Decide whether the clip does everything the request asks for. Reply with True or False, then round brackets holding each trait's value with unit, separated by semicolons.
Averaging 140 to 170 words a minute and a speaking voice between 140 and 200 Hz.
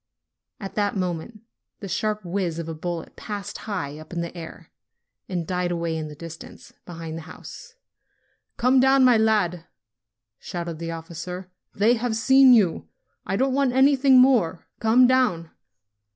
True (160 wpm; 190 Hz)